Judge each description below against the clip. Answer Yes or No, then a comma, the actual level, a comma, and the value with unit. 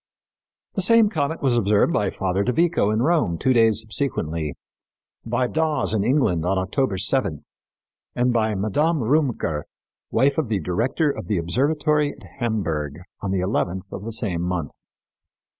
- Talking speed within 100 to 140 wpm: No, average, 160 wpm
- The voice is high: No, low, 110 Hz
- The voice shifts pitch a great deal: Yes, wide, 7.1 semitones